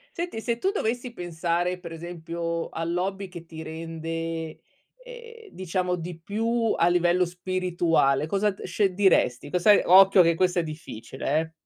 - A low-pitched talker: No, medium, 175 Hz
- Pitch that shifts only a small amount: No, average, 3.0 semitones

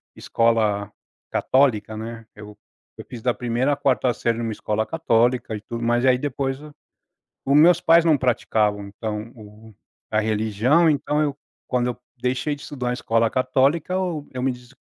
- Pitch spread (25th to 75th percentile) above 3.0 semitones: Yes, average, 3.9 semitones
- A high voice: No, low, 125 Hz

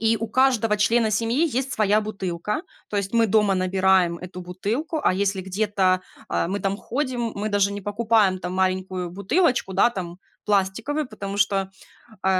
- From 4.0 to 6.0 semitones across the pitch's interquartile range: No, average, 3.2 semitones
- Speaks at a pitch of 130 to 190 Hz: No, high, 200 Hz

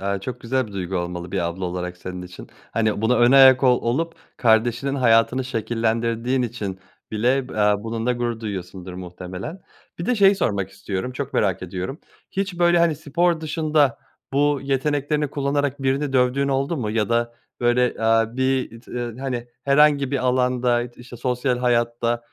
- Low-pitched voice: Yes, low, 120 Hz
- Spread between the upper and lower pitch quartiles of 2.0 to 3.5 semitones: No, average, 4.0 semitones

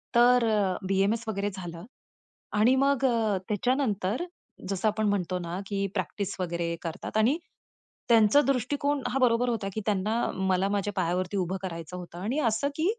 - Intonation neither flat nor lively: Yes, average, 4.6 semitones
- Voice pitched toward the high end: Yes, high, 205 Hz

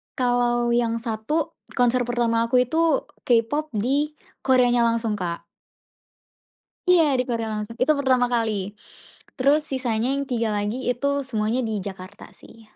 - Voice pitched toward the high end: Yes, high, 240 Hz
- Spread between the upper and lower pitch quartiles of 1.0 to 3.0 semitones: Yes, narrow, 2.6 semitones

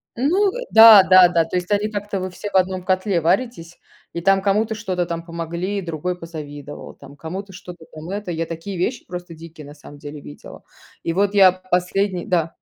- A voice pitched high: No, medium, 180 Hz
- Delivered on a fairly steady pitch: No, average, 3.1 semitones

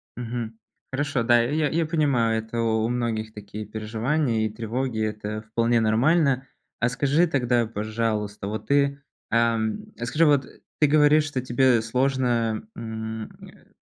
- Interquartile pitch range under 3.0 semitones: No, average, 3.6 semitones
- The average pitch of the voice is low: Yes, low, 120 Hz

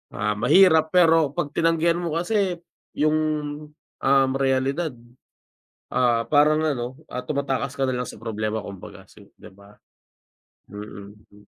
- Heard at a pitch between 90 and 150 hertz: Yes, medium, 140 Hz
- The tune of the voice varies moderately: No, wide, 6.1 semitones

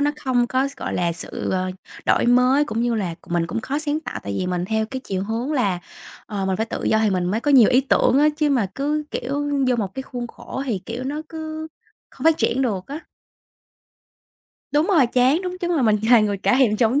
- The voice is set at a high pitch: Yes, high, 245 Hz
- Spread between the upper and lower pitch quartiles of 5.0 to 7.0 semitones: Yes, wide, 5.4 semitones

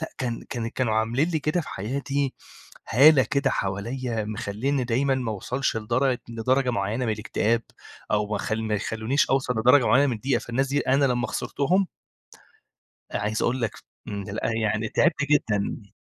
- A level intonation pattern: No, average, 3.8 semitones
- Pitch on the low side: Yes, low, 120 Hz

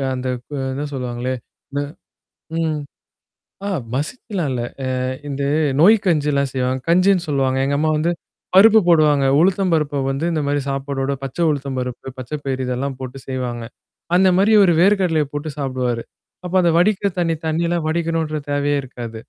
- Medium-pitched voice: Yes, medium, 145 Hz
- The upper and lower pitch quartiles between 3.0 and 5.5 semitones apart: Yes, average, 4.3 semitones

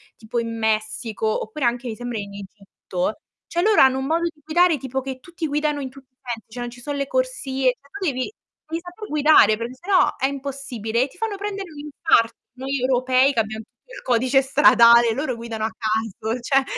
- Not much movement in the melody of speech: No, average, 4.5 semitones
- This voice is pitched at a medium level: No, very high, 260 Hz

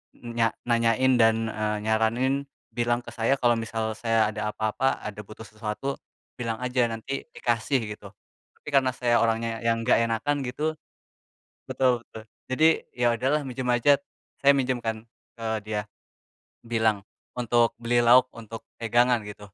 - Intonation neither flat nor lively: No, narrow, 2.1 semitones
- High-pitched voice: No, low, 115 Hz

